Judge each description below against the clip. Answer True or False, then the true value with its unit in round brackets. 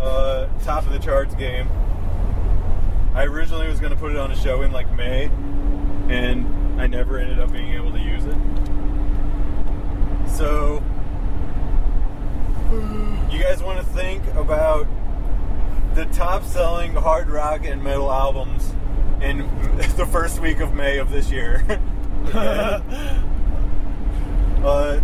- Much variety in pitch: True (8.2 semitones)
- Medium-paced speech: False (130 wpm)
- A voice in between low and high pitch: False (95 Hz)